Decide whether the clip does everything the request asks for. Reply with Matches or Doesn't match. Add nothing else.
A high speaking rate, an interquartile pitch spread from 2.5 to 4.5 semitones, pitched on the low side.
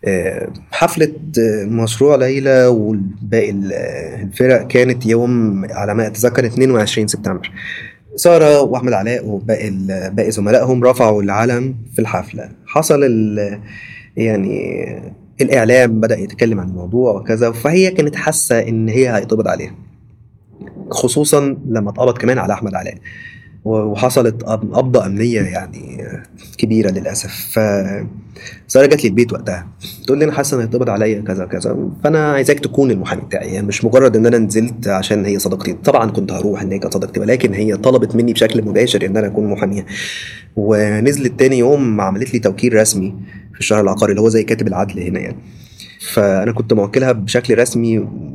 Matches